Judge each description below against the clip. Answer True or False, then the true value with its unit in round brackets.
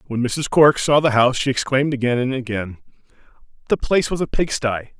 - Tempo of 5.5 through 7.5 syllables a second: True (6.0 syllables/s)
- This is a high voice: False (130 Hz)